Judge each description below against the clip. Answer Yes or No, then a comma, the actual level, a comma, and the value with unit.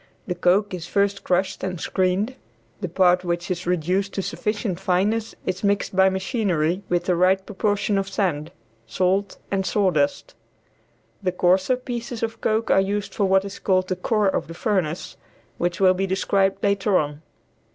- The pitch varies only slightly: Yes, narrow, 2.0 semitones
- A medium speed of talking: Yes, average, 170 wpm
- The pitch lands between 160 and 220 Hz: Yes, high, 190 Hz